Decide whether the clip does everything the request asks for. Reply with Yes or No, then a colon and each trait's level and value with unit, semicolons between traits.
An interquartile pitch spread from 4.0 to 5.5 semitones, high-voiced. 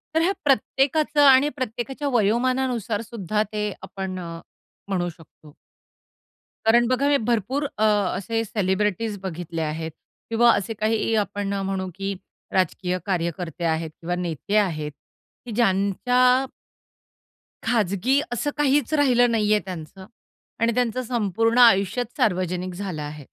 Yes: average, 4.9 semitones; high, 210 Hz